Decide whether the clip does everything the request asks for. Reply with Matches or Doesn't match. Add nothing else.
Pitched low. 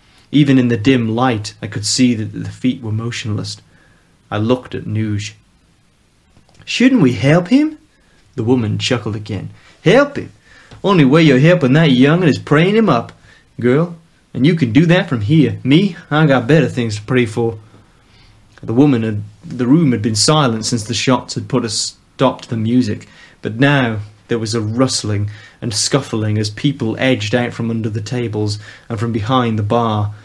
Matches